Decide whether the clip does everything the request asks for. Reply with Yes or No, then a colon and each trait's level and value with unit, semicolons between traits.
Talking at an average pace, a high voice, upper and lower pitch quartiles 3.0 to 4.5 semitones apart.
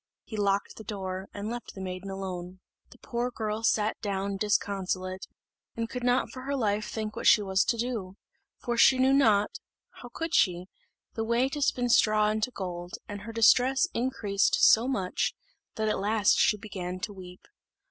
Yes: average, 180 wpm; high, 210 Hz; average, 3.7 semitones